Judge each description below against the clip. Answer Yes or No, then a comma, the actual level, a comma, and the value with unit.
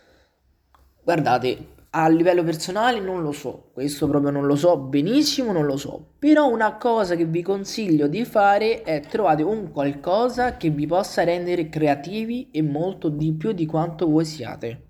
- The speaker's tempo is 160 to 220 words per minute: Yes, average, 165 wpm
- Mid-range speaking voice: Yes, medium, 170 Hz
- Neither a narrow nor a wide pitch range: No, wide, 5.8 semitones